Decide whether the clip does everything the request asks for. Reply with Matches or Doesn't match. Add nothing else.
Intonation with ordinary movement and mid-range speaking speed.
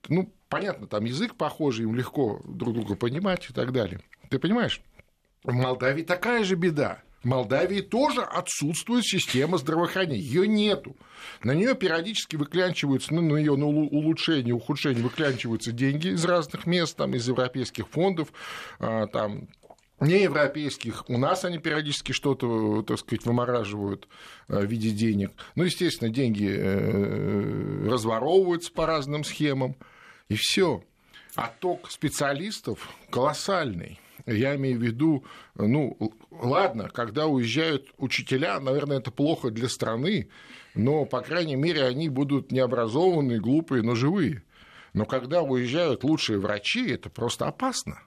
Doesn't match